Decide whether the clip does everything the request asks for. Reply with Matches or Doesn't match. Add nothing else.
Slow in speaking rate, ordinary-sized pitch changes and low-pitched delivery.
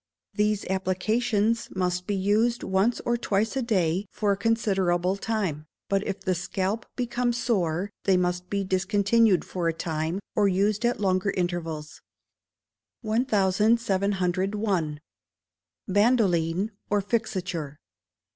Doesn't match